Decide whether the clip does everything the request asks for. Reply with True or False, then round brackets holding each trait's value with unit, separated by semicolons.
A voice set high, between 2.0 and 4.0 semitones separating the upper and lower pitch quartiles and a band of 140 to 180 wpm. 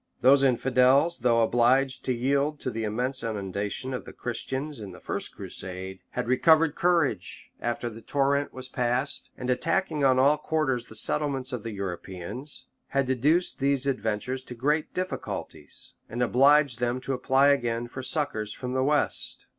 False (130 Hz; 3.0 semitones; 160 wpm)